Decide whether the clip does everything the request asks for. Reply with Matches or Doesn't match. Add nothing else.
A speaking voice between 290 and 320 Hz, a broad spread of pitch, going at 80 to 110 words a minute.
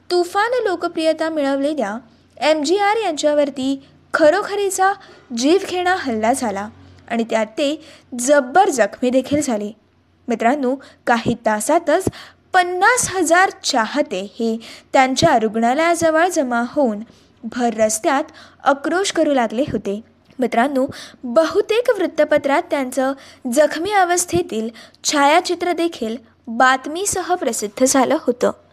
Matches